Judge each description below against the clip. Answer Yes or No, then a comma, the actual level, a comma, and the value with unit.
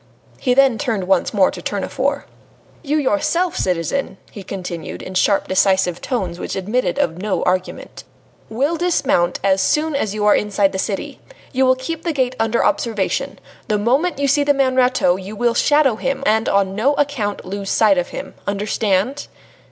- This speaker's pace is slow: No, average, 175 wpm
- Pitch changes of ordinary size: No, wide, 6.1 semitones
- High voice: Yes, high, 215 Hz